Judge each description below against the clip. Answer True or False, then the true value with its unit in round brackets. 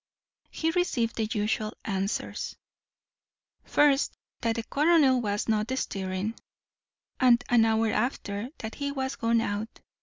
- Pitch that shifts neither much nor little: True (3.7 semitones)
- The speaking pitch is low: False (230 Hz)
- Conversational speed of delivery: False (125 wpm)